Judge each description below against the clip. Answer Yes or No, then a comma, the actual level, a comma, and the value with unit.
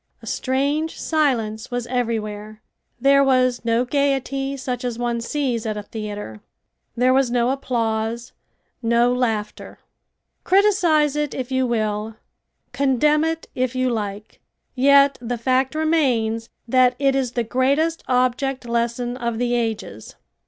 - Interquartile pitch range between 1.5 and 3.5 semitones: Yes, average, 3.0 semitones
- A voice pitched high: Yes, very high, 250 Hz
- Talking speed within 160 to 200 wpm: No, slow, 135 wpm